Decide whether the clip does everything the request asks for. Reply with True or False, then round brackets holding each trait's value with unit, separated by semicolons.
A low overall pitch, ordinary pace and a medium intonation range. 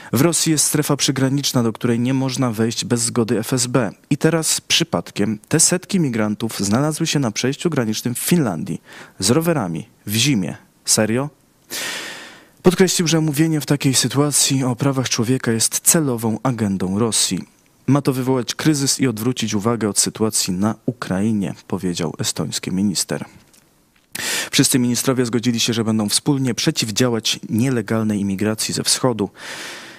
True (125 Hz; 140 wpm; 4.5 semitones)